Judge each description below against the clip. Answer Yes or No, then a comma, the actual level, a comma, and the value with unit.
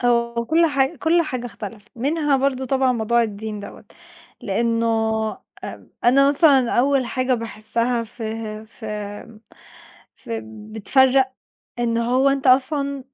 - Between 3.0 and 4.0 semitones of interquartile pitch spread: Yes, average, 3.4 semitones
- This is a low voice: No, high, 245 Hz